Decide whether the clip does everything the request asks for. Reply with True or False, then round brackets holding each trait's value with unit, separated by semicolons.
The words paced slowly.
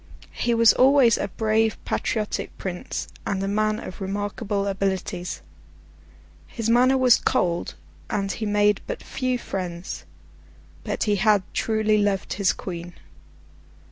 True (130 wpm)